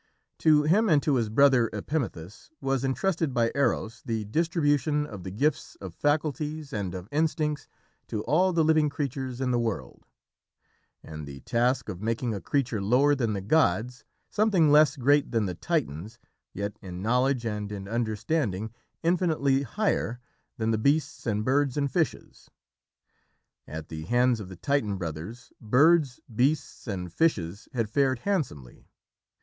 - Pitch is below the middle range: Yes, low, 125 Hz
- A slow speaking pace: No, average, 155 wpm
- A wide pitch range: Yes, wide, 5.9 semitones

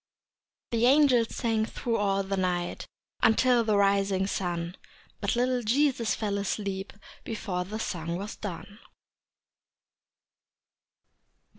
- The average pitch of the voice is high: Yes, high, 205 Hz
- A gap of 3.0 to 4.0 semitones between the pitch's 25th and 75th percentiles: Yes, average, 3.3 semitones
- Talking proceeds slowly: Yes, slow, 110 wpm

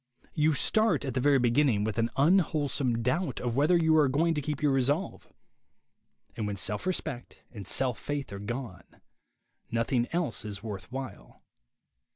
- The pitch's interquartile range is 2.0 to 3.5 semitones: No, average, 4.6 semitones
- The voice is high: No, low, 135 Hz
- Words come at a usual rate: Yes, average, 165 wpm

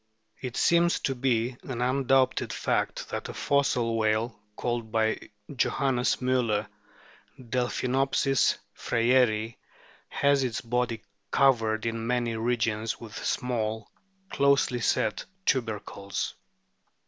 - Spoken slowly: Yes, slow, 100 wpm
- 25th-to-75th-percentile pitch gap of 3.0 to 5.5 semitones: No, narrow, 2.6 semitones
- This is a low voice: Yes, low, 120 Hz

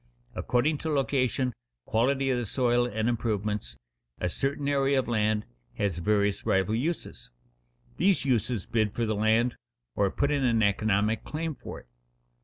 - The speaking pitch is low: Yes, low, 120 Hz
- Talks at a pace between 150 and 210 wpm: Yes, average, 155 wpm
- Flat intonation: No, average, 4.3 semitones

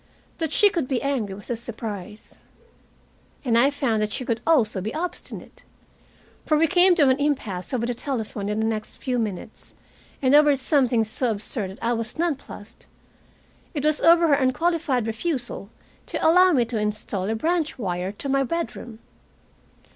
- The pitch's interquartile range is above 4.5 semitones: Yes, wide, 5.4 semitones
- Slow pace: No, average, 175 wpm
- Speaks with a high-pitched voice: Yes, very high, 250 Hz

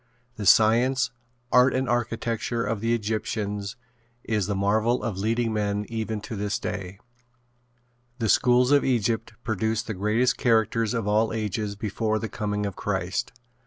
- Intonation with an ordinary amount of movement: No, narrow, 2.1 semitones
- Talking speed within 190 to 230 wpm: No, average, 150 wpm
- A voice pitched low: Yes, low, 110 Hz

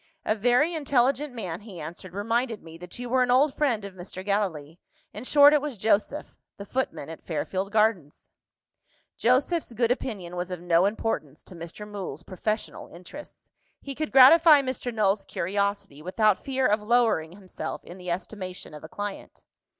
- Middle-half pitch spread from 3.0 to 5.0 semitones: No, wide, 5.6 semitones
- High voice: Yes, high, 210 Hz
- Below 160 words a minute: No, average, 170 wpm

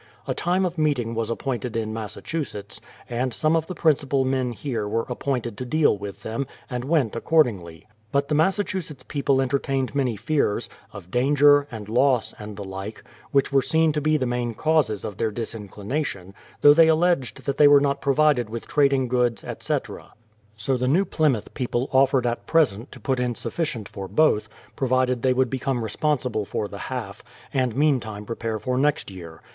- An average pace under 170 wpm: No, average, 185 wpm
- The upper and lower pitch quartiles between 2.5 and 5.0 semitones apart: Yes, average, 4.4 semitones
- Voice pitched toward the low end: Yes, low, 130 Hz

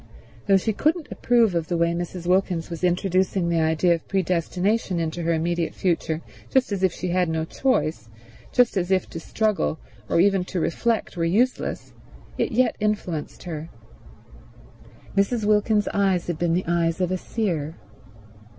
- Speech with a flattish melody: No, average, 3.4 semitones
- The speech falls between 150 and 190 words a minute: Yes, average, 165 wpm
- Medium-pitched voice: Yes, medium, 180 Hz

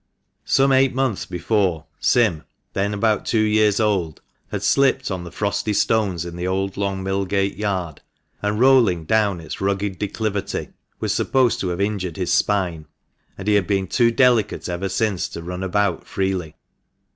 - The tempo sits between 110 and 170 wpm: Yes, average, 165 wpm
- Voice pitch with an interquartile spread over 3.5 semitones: No, average, 2.9 semitones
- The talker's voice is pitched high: No, low, 100 Hz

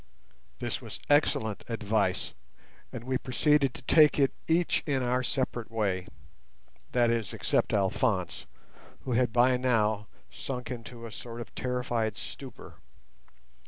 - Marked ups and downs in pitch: No, average, 3.0 semitones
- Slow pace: Yes, slow, 125 wpm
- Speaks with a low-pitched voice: Yes, low, 120 Hz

